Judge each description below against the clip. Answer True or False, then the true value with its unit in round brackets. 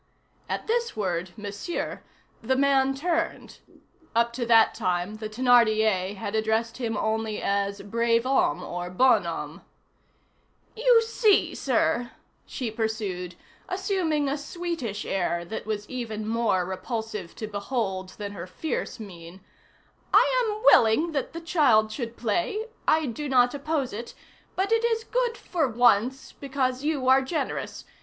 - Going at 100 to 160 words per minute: True (140 wpm)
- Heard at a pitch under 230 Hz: False (235 Hz)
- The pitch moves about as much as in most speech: False (5.9 semitones)